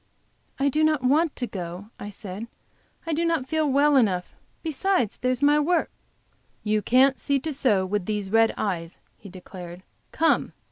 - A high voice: Yes, very high, 250 Hz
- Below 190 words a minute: Yes, average, 170 wpm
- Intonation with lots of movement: Yes, wide, 6.9 semitones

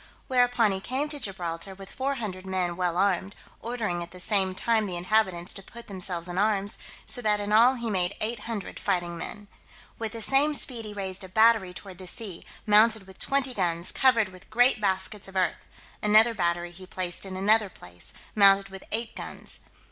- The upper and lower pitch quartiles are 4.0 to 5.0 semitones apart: No, average, 3.3 semitones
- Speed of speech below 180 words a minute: No, average, 195 wpm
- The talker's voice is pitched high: Yes, high, 200 Hz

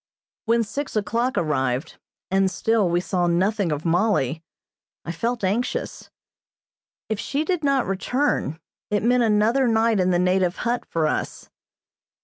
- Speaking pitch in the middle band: No, high, 205 Hz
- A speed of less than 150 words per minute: Yes, average, 140 wpm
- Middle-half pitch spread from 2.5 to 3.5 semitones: No, average, 5.1 semitones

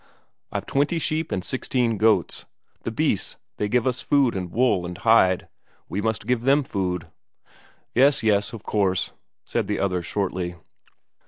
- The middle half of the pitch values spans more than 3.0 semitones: Yes, average, 5.3 semitones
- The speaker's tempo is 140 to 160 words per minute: Yes, average, 155 wpm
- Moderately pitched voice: No, low, 110 Hz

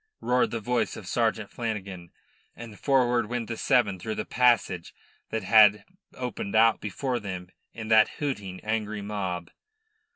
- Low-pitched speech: Yes, low, 110 Hz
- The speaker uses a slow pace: No, average, 150 wpm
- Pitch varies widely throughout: No, average, 3.1 semitones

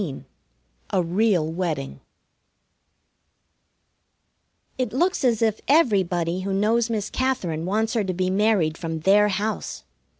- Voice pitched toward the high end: Yes, high, 200 Hz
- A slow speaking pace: Yes, slow, 125 wpm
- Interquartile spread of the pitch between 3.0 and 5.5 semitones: Yes, average, 4.4 semitones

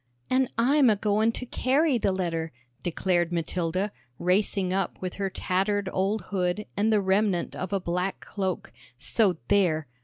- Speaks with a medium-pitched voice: No, high, 195 Hz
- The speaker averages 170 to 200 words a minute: No, average, 155 wpm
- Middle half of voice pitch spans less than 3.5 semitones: Yes, average, 2.8 semitones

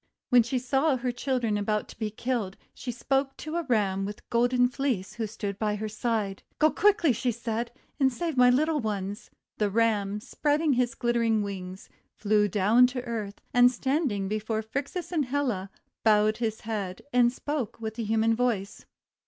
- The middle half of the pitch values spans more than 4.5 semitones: No, average, 3.4 semitones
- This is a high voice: Yes, high, 230 Hz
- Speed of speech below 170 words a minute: No, average, 175 wpm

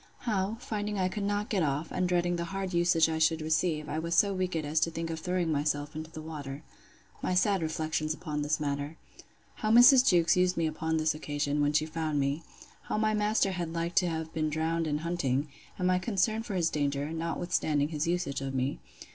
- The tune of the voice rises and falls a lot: No, average, 3.0 semitones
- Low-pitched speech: No, medium, 165 Hz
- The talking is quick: Yes, fast, 215 wpm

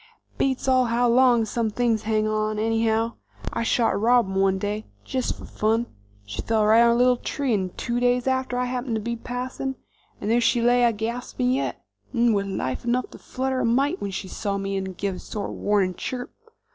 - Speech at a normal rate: No, fast, 215 wpm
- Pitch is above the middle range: Yes, high, 230 Hz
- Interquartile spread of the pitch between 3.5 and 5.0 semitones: No, average, 2.8 semitones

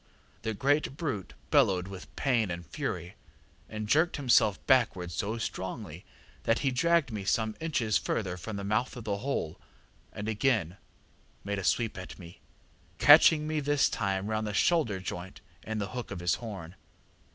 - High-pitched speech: No, low, 110 Hz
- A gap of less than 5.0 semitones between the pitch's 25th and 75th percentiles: No, average, 5.3 semitones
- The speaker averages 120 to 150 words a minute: No, average, 165 wpm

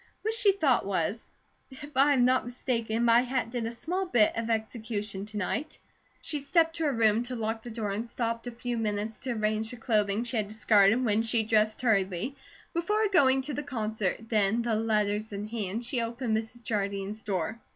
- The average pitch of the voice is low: No, high, 230 Hz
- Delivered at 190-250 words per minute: Yes, fast, 205 wpm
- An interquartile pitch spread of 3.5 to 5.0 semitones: No, average, 3.0 semitones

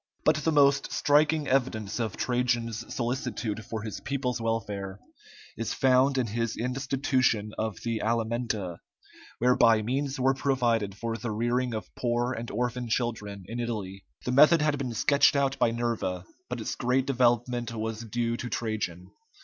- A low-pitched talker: Yes, low, 120 Hz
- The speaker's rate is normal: Yes, average, 155 wpm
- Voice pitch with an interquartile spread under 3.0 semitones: Yes, narrow, 2.5 semitones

